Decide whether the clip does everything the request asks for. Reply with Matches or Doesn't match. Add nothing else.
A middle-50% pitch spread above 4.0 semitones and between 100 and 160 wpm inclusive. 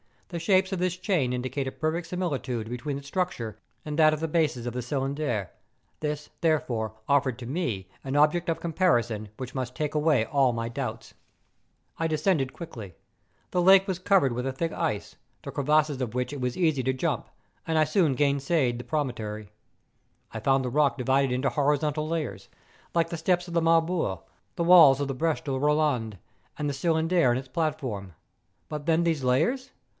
Doesn't match